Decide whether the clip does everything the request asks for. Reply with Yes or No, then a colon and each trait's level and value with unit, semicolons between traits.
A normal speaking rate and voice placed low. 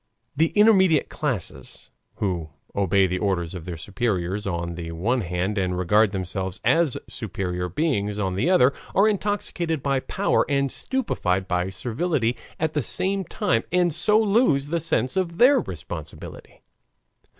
Yes: average, 150 wpm; low, 115 Hz